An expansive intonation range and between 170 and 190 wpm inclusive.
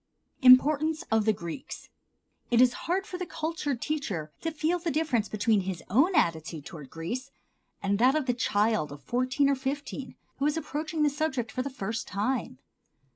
Yes: wide, 6.3 semitones; average, 180 wpm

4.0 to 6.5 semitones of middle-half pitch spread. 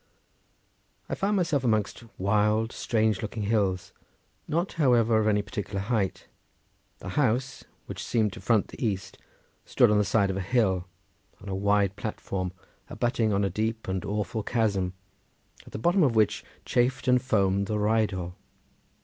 No: average, 3.2 semitones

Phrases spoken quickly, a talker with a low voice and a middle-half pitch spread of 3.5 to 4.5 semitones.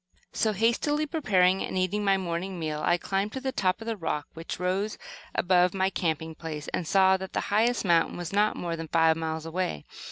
No: fast, 210 wpm; medium, 185 Hz; average, 3.8 semitones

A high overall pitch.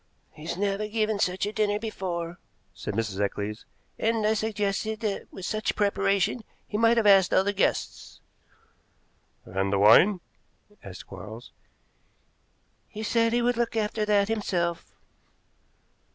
Yes: high, 205 Hz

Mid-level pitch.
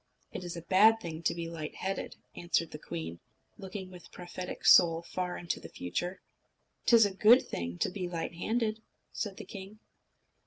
Yes: medium, 180 Hz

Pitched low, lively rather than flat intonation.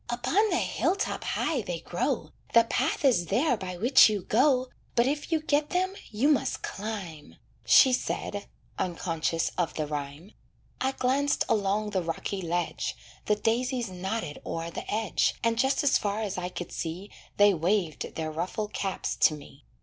No: high, 210 Hz; wide, 6.4 semitones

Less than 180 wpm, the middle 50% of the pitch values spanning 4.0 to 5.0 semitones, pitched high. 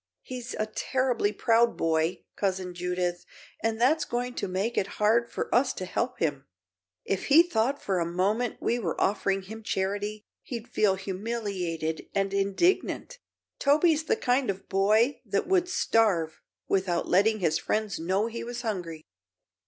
Yes: average, 155 wpm; average, 4.4 semitones; high, 210 Hz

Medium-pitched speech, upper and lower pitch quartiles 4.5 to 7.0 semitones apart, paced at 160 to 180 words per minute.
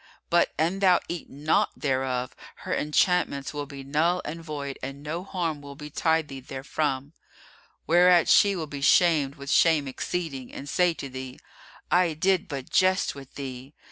No: medium, 150 Hz; average, 3.8 semitones; average, 165 wpm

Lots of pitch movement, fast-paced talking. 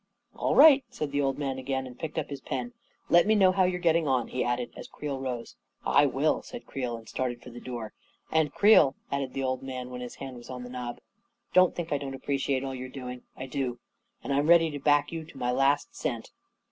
No: average, 3.2 semitones; fast, 255 wpm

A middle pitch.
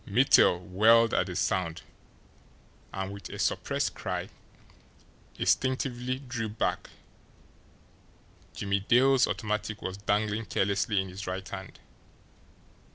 No: low, 100 Hz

